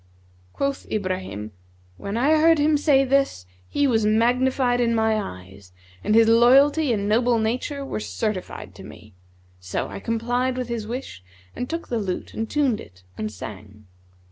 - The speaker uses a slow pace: No, average, 165 wpm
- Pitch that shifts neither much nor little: Yes, average, 4.8 semitones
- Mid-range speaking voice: No, high, 230 Hz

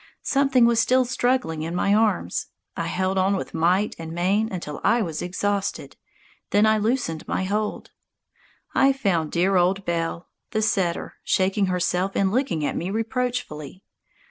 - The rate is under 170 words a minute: Yes, average, 155 wpm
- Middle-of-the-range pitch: No, high, 195 Hz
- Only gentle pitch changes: No, average, 4.2 semitones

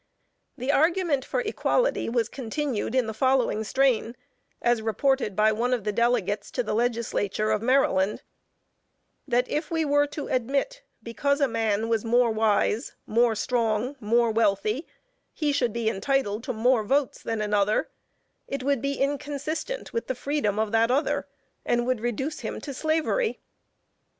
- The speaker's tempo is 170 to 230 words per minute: No, average, 155 wpm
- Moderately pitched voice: No, high, 240 Hz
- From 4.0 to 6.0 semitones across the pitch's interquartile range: Yes, average, 4.3 semitones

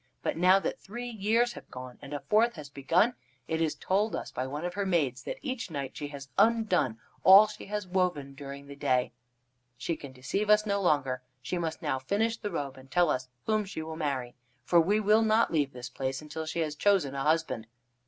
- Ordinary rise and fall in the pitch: No, wide, 6.8 semitones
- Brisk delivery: Yes, fast, 220 wpm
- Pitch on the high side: No, medium, 160 Hz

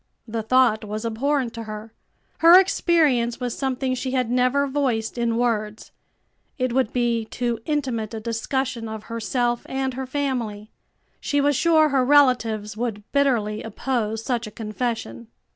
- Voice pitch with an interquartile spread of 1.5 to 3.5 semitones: Yes, average, 3.2 semitones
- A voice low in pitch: No, high, 240 Hz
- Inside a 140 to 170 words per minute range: Yes, average, 150 wpm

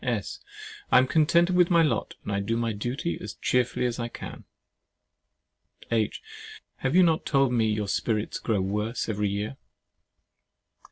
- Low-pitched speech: Yes, low, 120 Hz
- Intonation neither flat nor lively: Yes, average, 4.5 semitones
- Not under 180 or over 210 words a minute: No, average, 155 wpm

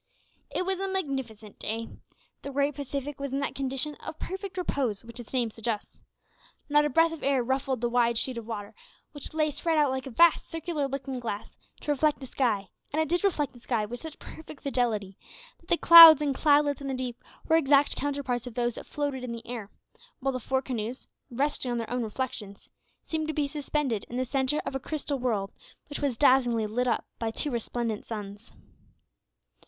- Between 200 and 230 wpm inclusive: Yes, fast, 205 wpm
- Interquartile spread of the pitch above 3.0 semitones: Yes, average, 3.8 semitones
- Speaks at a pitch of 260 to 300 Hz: Yes, very high, 265 Hz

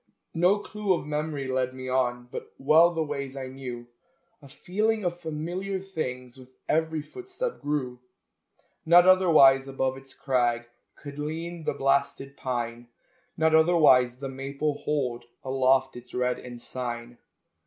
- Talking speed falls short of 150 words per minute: Yes, average, 140 wpm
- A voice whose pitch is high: No, medium, 140 Hz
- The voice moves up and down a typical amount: Yes, average, 4.1 semitones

